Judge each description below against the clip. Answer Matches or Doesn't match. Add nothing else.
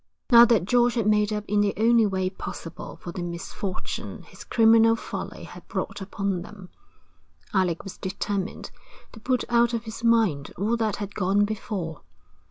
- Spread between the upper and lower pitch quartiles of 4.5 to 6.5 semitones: Doesn't match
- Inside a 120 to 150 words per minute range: Doesn't match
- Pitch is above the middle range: Matches